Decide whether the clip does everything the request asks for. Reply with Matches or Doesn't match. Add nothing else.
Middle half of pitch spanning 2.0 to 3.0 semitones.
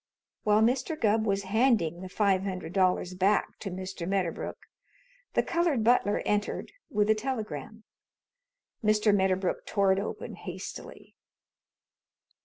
Matches